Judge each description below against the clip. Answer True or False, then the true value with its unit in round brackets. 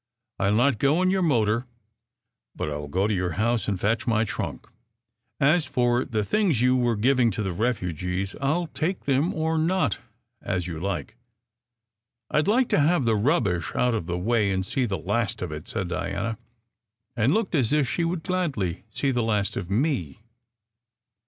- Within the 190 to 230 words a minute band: True (195 wpm)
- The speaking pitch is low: True (115 Hz)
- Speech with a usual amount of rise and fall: False (6.3 semitones)